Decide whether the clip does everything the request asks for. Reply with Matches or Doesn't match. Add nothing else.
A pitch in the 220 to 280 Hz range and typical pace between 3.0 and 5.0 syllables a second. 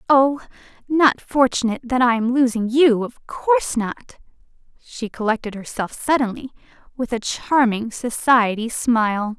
Matches